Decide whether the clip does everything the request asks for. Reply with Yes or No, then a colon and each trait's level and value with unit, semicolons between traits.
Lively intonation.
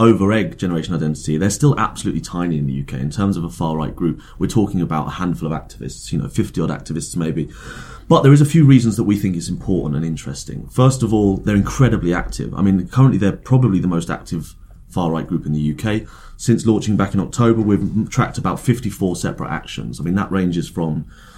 No: average, 4.7 semitones